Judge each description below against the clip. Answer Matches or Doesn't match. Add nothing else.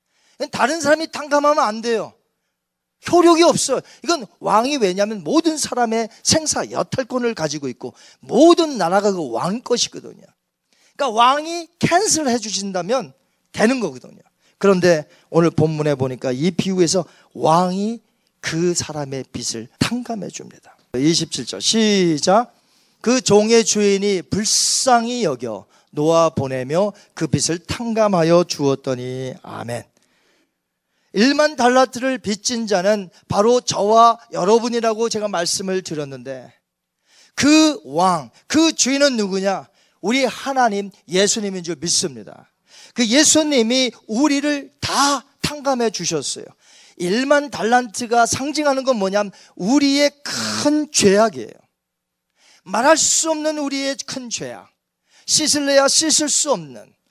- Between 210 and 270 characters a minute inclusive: Matches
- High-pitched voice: Matches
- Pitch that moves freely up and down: Matches